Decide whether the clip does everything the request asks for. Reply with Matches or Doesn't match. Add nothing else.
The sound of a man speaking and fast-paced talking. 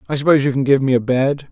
Matches